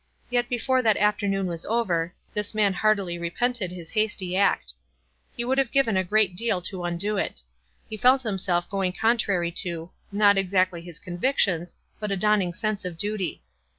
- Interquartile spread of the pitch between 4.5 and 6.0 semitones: No, average, 3.4 semitones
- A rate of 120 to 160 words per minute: No, average, 180 wpm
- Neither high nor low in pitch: No, high, 195 Hz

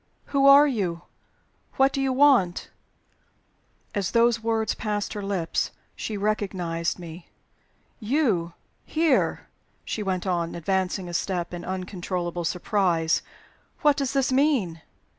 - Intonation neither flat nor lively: No, wide, 6.5 semitones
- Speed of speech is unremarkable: No, slow, 125 wpm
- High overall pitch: Yes, high, 200 Hz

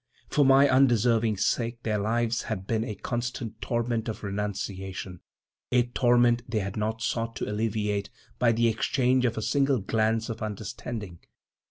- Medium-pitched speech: No, low, 115 Hz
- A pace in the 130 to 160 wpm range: Yes, average, 150 wpm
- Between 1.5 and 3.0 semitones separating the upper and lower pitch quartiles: Yes, narrow, 2.4 semitones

